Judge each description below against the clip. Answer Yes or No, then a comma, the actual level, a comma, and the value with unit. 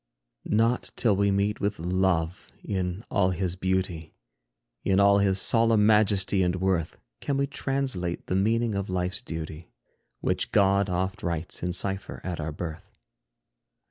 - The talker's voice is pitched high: No, very low, 95 Hz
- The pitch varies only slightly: Yes, narrow, 2.3 semitones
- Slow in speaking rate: No, average, 145 wpm